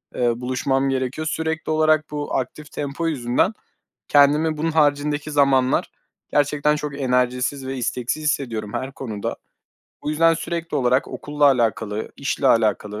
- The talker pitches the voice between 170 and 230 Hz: No, medium, 140 Hz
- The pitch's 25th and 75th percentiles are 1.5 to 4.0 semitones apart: Yes, average, 3.2 semitones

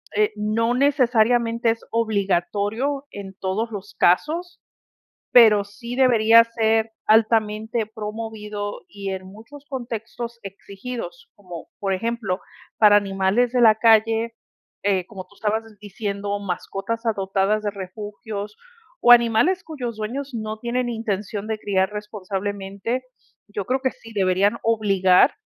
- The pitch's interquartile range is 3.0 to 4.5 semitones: No, narrow, 2.6 semitones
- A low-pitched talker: No, high, 215 Hz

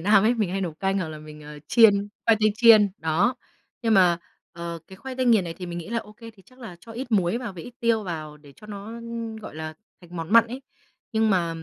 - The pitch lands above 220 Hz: No, high, 200 Hz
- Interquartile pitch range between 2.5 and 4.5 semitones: No, average, 5.0 semitones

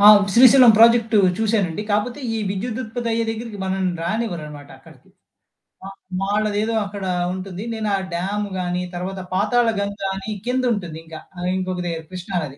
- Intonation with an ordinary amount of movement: Yes, average, 3.5 semitones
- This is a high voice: Yes, high, 205 Hz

